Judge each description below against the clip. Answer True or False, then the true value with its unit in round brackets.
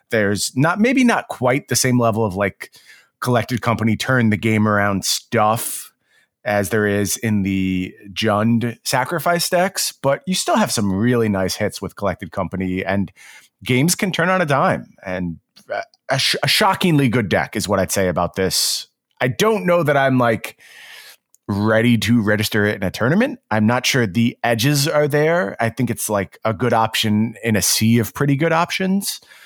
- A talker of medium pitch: False (115 Hz)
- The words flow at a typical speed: True (180 wpm)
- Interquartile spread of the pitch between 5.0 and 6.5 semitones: True (5.3 semitones)